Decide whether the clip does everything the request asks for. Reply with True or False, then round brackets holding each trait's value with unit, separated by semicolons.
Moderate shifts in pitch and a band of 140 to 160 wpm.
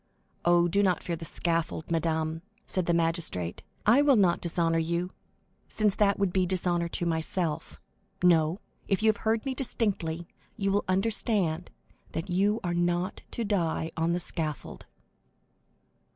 True (3.2 semitones; 150 wpm)